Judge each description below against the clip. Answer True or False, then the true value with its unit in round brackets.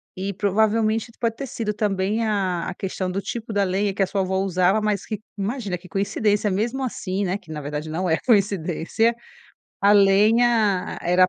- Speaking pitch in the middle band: False (200 Hz)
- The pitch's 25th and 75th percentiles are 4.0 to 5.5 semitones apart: False (2.7 semitones)